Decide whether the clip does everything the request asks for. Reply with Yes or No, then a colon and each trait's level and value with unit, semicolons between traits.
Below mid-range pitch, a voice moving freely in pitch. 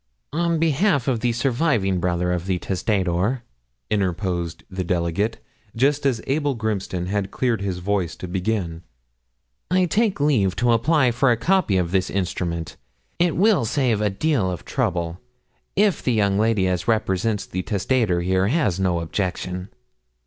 Yes: low, 100 Hz; wide, 6.1 semitones